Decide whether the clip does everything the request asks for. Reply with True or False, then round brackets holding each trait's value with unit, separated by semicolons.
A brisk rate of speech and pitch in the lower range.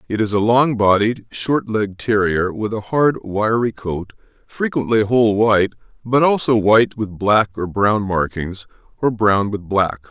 False (165 wpm; 110 Hz)